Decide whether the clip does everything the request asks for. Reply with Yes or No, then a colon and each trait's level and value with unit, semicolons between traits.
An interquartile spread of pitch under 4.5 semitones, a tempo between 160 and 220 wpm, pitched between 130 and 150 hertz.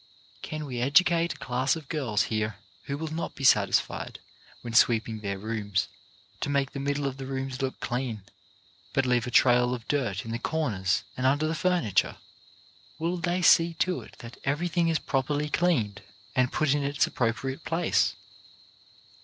No: average, 4.8 semitones; average, 180 wpm; low, 135 Hz